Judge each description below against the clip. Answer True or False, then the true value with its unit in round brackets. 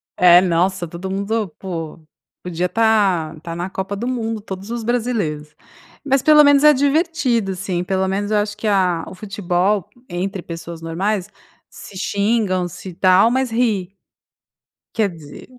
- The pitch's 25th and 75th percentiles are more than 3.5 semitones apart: True (4.1 semitones)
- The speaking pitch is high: True (195 Hz)